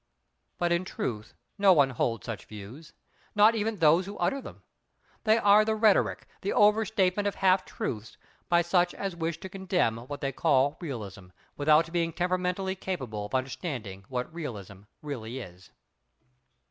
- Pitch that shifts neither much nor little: No, wide, 7.4 semitones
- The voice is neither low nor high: Yes, medium, 165 Hz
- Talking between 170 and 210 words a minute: No, average, 160 wpm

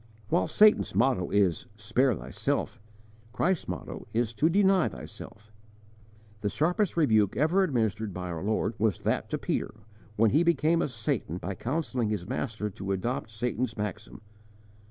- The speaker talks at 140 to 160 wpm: Yes, average, 150 wpm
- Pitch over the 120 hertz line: No, low, 110 Hz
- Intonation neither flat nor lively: No, wide, 6.6 semitones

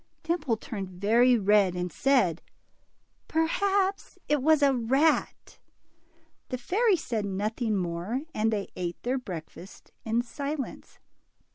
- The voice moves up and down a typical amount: No, wide, 6.5 semitones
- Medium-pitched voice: No, high, 235 Hz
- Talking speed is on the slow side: Yes, slow, 120 wpm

